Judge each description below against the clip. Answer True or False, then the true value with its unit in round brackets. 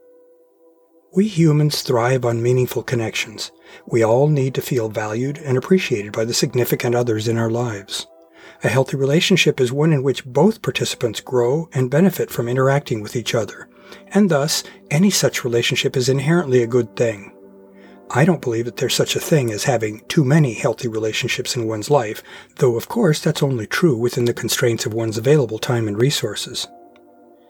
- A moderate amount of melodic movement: True (4.3 semitones)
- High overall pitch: False (130 Hz)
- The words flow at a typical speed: True (175 wpm)